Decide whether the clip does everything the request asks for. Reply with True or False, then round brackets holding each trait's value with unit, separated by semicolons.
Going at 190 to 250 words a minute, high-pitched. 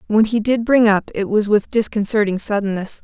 True (200 wpm; 210 Hz)